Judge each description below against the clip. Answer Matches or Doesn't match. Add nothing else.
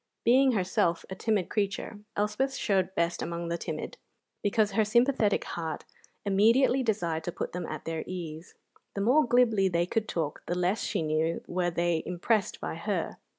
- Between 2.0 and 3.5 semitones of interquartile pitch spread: Doesn't match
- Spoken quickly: Doesn't match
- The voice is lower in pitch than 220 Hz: Matches